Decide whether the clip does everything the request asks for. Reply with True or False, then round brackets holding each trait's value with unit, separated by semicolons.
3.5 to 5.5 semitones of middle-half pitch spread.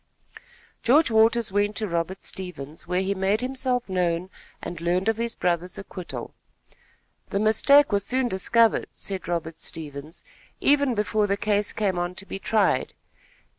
True (3.9 semitones)